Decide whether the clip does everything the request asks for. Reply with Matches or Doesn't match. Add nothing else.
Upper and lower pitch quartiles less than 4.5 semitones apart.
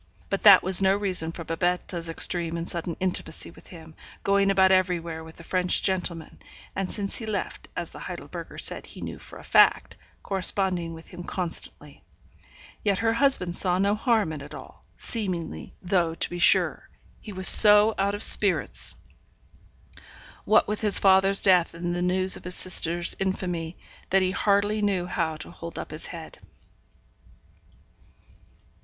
Matches